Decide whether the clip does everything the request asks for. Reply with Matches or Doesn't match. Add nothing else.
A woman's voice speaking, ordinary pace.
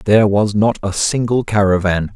Doesn't match